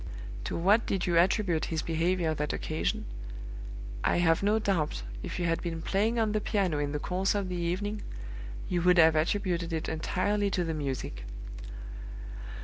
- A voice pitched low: No, medium, 175 Hz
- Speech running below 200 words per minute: Yes, average, 170 wpm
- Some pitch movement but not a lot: Yes, average, 3.6 semitones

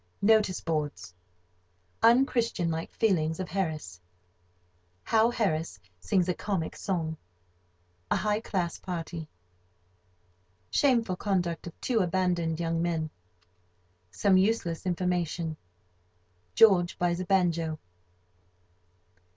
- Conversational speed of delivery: No, slow, 75 wpm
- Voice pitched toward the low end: No, medium, 160 Hz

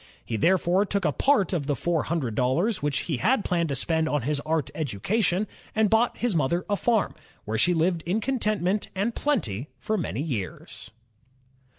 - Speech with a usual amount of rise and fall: No, wide, 6.5 semitones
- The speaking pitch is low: No, medium, 170 Hz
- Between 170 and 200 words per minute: Yes, average, 185 wpm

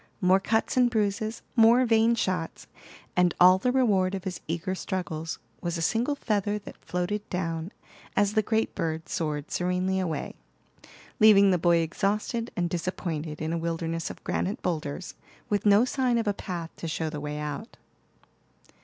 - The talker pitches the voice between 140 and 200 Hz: Yes, medium, 185 Hz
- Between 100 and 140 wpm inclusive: No, average, 165 wpm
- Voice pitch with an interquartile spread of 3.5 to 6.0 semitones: Yes, average, 4.3 semitones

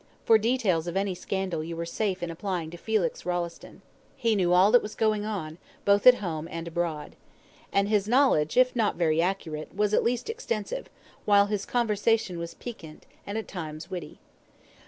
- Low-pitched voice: No, high, 195 Hz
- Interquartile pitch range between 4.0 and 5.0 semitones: Yes, average, 4.4 semitones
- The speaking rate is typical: Yes, average, 180 wpm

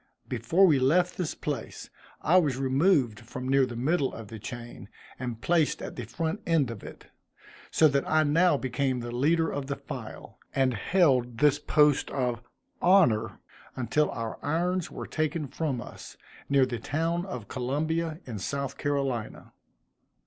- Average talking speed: Yes, average, 160 wpm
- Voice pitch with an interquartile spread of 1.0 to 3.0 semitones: No, average, 4.6 semitones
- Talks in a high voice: No, medium, 140 Hz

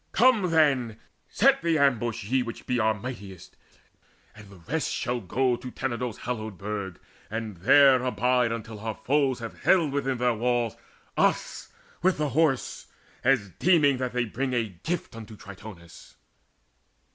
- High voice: No, low, 125 Hz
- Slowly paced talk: No, average, 150 wpm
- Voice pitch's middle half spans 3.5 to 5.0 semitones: Yes, average, 3.8 semitones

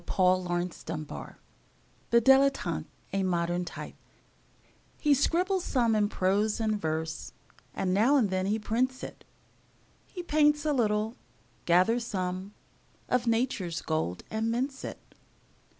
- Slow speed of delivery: Yes, slow, 130 wpm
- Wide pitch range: Yes, wide, 5.9 semitones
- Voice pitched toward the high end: Yes, high, 215 Hz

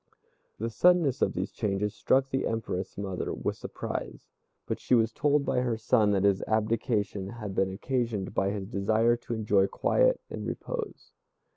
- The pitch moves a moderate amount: Yes, average, 4.0 semitones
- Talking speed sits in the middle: Yes, average, 165 wpm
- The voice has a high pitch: No, low, 110 Hz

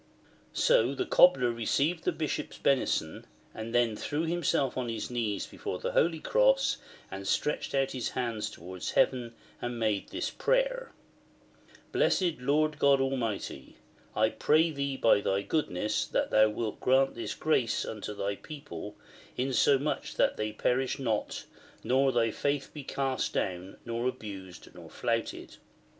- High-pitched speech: No, low, 125 Hz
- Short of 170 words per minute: Yes, average, 150 wpm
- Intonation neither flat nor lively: Yes, average, 4.9 semitones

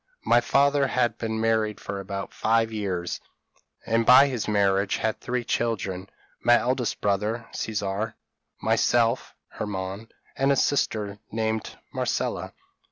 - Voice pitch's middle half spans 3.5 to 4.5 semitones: No, average, 2.9 semitones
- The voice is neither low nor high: No, low, 110 Hz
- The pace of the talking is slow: Yes, slow, 125 wpm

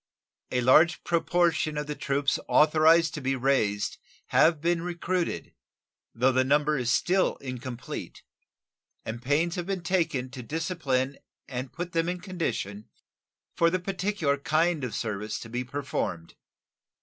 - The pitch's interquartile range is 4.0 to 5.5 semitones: Yes, average, 4.9 semitones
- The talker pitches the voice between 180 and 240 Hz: No, medium, 150 Hz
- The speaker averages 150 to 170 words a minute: No, average, 140 wpm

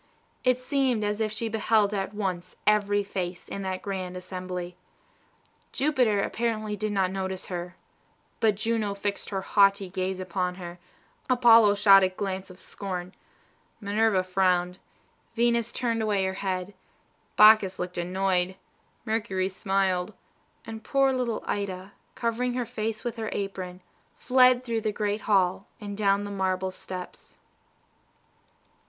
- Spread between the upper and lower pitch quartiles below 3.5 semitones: Yes, average, 2.9 semitones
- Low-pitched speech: No, high, 200 Hz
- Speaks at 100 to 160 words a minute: Yes, slow, 135 wpm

